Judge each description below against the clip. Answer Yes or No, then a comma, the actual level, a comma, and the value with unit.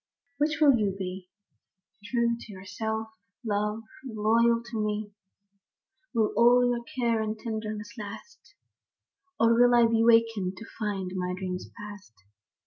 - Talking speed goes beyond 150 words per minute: No, average, 145 wpm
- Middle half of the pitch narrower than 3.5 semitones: Yes, narrow, 2.5 semitones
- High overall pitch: Yes, high, 220 Hz